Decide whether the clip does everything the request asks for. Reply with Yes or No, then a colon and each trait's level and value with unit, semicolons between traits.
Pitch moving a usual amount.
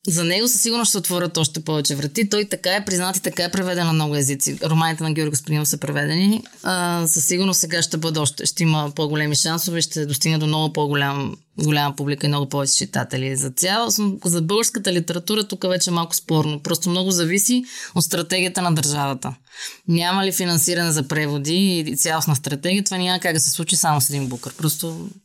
Yes: average, 3.4 semitones